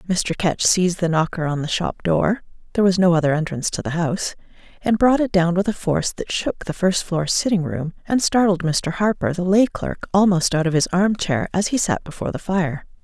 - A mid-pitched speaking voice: Yes, medium, 180 Hz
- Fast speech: Yes, fast, 215 wpm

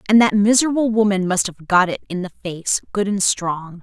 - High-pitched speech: Yes, high, 200 Hz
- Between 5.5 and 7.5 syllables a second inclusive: No, 5.2 syllables/s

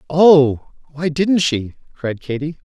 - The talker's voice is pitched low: No, medium, 150 Hz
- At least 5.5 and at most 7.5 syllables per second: No, 3.4 syllables/s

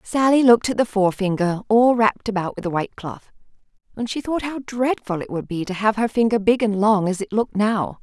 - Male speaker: No, female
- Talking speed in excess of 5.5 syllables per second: Yes, 5.8 syllables/s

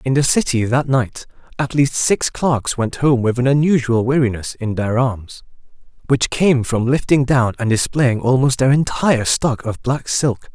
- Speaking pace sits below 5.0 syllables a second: Yes, 4.5 syllables/s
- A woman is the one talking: No, male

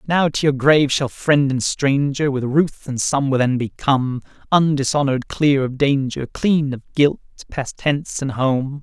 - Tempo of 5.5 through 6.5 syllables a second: No, 4.6 syllables/s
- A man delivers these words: Yes, male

